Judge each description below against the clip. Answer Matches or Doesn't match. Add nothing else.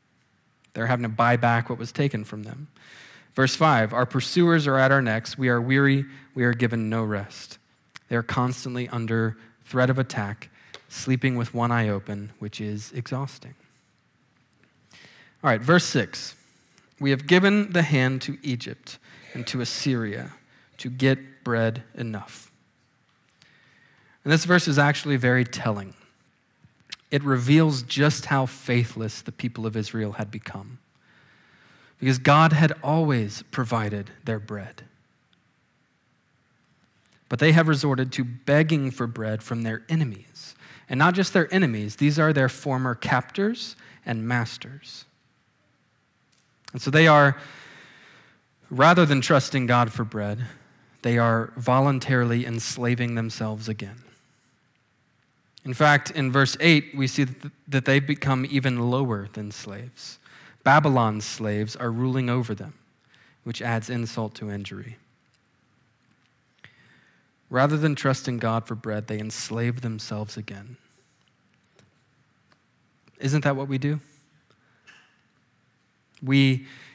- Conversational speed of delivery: Doesn't match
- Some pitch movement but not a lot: Matches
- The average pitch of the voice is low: Matches